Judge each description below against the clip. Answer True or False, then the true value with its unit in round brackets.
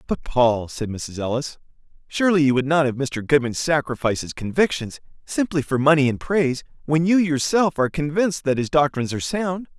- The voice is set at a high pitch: False (145 Hz)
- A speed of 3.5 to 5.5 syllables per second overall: False (5.7 syllables/s)